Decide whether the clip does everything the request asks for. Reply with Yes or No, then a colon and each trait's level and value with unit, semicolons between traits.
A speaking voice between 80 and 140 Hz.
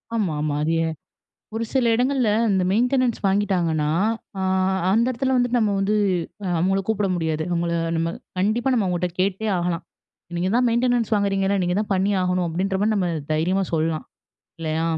No: high, 195 Hz